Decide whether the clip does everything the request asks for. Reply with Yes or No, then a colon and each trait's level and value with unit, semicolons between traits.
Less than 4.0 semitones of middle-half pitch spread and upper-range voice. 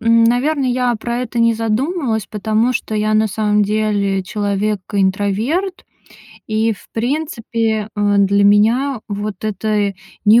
Yes: narrow, 2.5 semitones; high, 220 Hz